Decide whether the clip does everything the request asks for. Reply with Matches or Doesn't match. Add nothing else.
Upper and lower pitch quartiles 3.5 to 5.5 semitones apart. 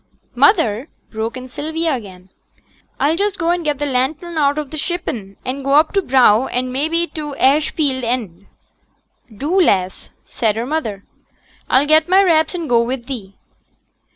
Matches